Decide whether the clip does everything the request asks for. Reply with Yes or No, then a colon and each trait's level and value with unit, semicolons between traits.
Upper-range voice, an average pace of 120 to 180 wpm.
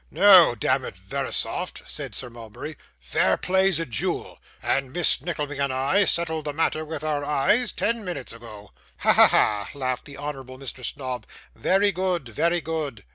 No: medium, 150 Hz; average, 170 wpm